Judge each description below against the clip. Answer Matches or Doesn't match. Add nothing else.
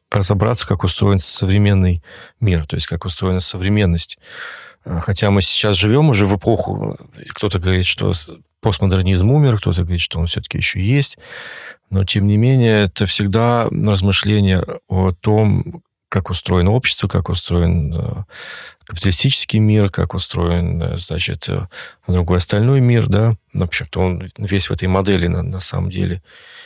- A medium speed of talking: Matches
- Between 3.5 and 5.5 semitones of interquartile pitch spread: Doesn't match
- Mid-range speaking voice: Doesn't match